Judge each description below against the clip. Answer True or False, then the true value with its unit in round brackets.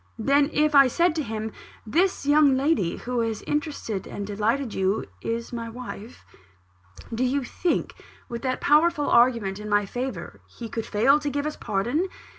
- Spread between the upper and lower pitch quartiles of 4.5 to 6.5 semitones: True (4.9 semitones)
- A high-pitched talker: True (250 Hz)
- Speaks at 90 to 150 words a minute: False (180 wpm)